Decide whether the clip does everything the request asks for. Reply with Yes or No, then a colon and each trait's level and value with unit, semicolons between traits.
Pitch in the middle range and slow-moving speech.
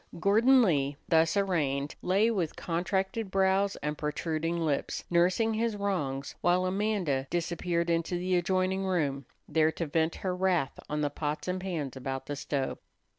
No: medium, 175 Hz; average, 155 wpm